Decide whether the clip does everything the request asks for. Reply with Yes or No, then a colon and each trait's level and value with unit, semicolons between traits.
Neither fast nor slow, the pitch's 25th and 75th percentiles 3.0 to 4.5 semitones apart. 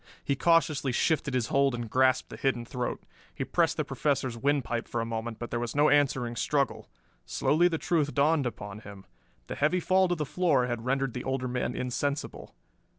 Yes: average, 195 wpm; average, 3.5 semitones